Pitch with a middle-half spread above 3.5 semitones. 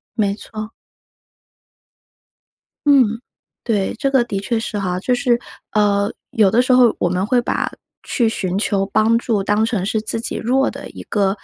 No: average, 3.0 semitones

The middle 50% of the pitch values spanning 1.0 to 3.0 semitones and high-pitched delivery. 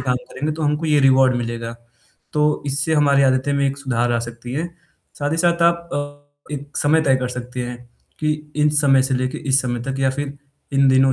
No: narrow, 2.6 semitones; low, 135 Hz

